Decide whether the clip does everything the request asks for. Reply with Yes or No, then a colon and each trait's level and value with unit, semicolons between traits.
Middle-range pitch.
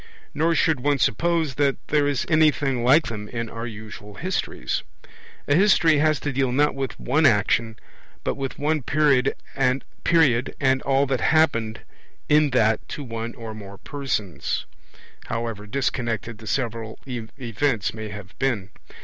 No: low, 130 Hz